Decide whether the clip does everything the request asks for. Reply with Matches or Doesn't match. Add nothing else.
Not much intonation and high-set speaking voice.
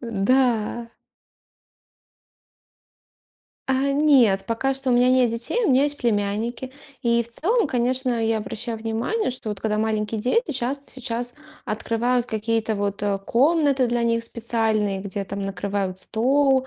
Doesn't match